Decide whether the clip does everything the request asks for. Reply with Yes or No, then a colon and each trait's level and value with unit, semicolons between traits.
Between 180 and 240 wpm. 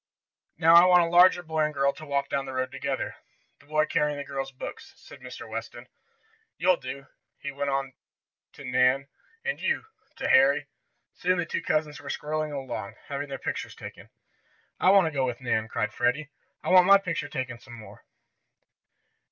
Yes: average, 185 wpm